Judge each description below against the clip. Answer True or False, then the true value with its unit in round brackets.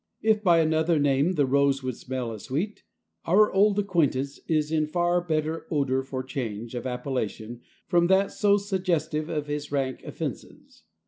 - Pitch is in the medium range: True (150 Hz)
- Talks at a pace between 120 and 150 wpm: False (165 wpm)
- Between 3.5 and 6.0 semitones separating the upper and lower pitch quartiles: True (4.9 semitones)